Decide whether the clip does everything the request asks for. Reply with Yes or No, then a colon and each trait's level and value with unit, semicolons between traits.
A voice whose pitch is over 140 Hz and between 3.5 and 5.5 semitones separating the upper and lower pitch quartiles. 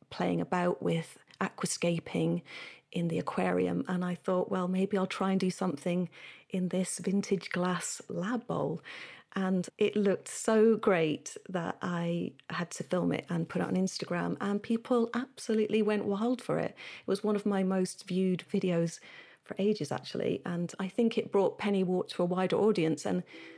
No: medium, 185 Hz; average, 2.8 semitones